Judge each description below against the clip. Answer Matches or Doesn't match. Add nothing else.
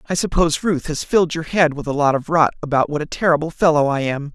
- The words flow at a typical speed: Doesn't match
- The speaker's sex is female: Doesn't match